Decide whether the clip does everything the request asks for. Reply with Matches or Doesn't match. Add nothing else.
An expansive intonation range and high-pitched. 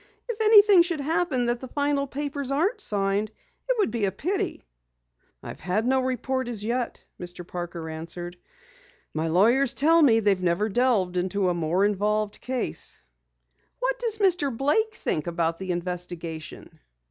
Matches